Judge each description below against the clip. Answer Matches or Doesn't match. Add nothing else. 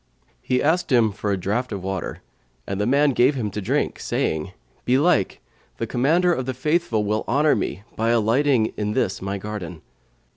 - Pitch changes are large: Doesn't match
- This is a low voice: Matches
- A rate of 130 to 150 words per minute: Doesn't match